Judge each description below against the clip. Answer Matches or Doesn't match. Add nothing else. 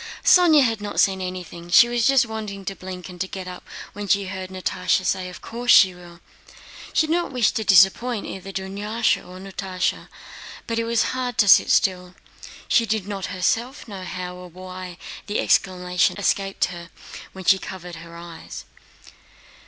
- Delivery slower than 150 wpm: Doesn't match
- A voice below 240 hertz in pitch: Matches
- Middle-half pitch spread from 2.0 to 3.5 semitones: Matches